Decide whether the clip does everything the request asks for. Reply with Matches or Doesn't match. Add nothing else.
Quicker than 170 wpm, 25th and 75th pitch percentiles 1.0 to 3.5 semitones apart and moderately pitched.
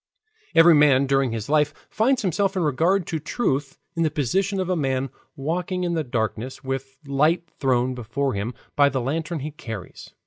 Doesn't match